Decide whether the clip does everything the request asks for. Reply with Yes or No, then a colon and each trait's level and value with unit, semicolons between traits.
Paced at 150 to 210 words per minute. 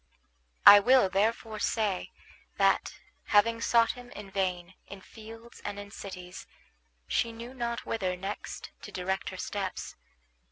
No: slow, 135 wpm